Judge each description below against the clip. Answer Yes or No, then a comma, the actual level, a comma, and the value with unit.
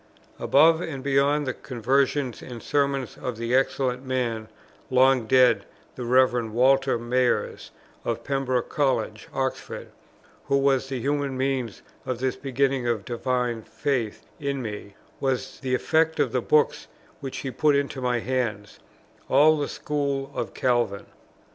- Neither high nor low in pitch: No, low, 130 Hz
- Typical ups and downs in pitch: No, narrow, 2.3 semitones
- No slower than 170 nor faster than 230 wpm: No, average, 145 wpm